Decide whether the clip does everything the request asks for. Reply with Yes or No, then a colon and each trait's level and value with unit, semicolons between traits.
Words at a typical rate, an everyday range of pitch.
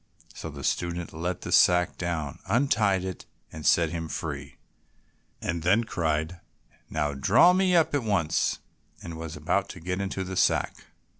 Yes: average, 160 wpm; average, 3.5 semitones